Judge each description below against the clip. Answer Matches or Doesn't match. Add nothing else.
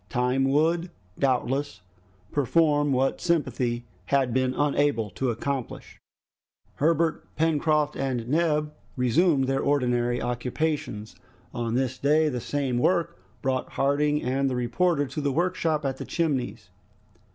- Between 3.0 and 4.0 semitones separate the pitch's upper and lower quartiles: Matches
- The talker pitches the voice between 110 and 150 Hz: Matches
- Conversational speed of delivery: Doesn't match